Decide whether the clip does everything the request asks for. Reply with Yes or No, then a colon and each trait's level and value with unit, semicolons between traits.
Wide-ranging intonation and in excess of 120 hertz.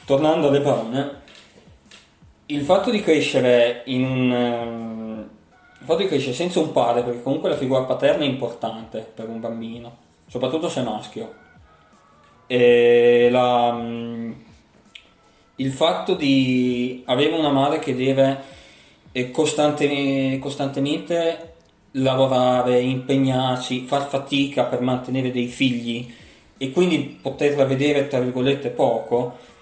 No: average, 2.7 semitones; low, 130 Hz